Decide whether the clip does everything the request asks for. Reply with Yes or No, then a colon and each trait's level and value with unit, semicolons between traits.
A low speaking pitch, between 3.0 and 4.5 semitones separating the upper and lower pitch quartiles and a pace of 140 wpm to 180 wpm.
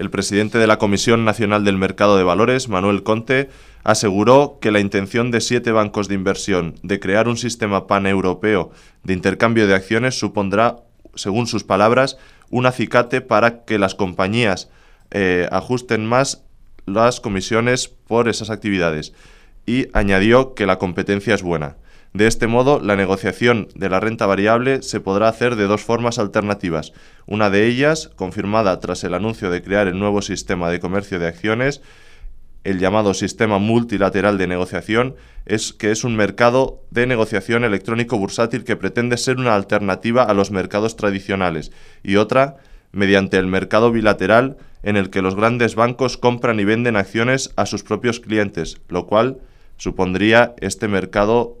Yes: low, 105 Hz; average, 3.3 semitones; average, 160 wpm